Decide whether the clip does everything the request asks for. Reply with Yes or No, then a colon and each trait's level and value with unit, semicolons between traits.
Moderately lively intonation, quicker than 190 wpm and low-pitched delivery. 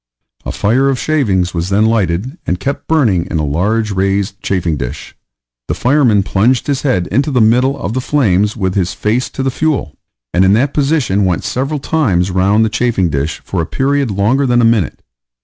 No: wide, 6.0 semitones; average, 200 wpm; low, 110 Hz